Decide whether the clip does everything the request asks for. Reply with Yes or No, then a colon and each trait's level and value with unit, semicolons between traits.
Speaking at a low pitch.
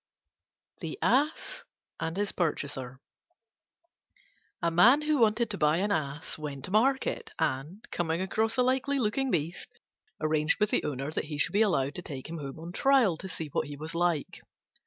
No: medium, 175 Hz